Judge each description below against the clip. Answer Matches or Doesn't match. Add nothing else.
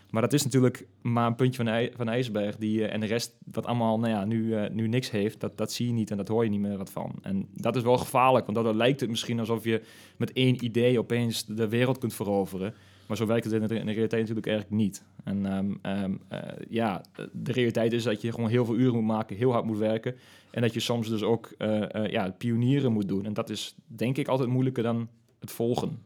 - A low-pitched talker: Matches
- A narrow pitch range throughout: Matches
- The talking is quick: Matches